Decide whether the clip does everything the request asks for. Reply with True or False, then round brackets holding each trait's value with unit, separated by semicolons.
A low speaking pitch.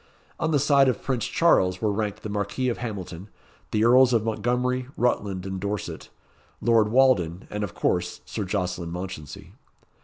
True (105 Hz)